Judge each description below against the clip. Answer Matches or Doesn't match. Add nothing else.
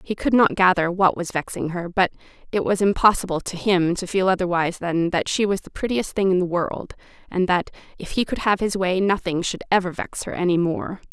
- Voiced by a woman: Matches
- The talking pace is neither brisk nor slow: Doesn't match